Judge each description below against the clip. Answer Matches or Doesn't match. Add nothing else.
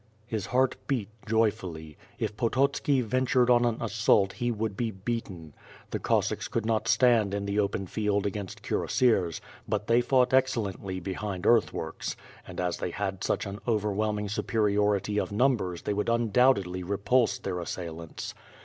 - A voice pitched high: Doesn't match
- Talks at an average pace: Matches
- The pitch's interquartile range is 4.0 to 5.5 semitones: Doesn't match